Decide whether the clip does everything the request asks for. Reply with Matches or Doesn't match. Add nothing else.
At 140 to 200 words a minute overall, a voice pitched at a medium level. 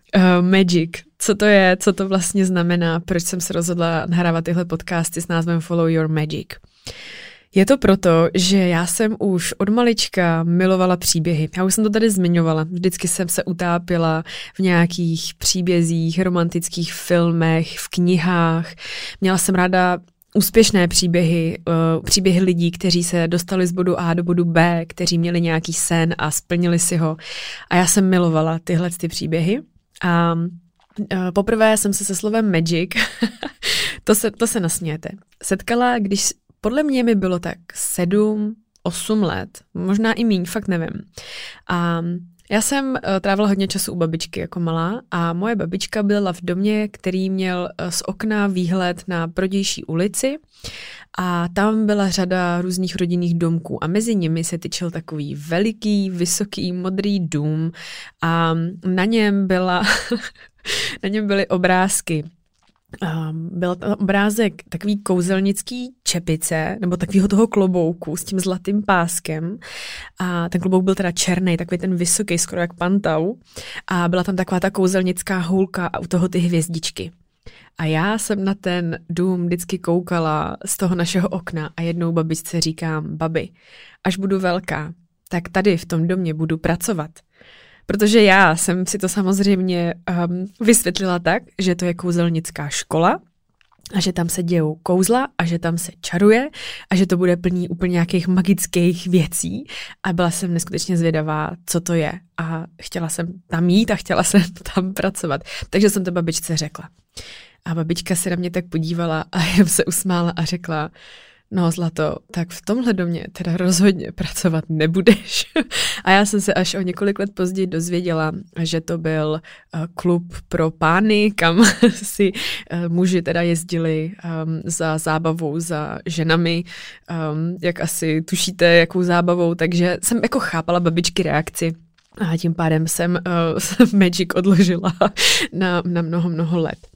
Matches